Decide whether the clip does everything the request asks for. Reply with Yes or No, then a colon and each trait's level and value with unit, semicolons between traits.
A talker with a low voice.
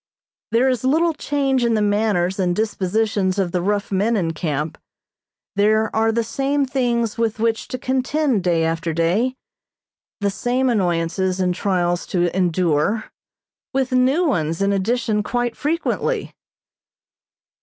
No: high, 210 Hz